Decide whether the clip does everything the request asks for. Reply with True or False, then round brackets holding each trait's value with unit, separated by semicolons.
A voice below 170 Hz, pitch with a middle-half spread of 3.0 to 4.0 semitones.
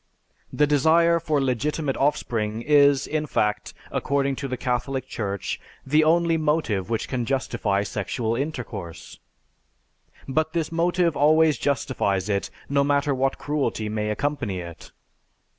False (140 Hz; 5.3 semitones)